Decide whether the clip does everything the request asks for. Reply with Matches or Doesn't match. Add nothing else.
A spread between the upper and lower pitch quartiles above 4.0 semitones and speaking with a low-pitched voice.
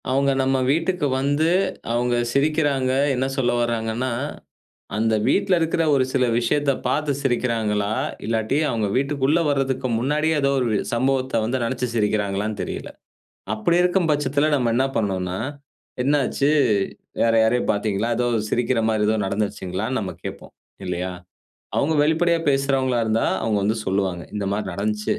Matches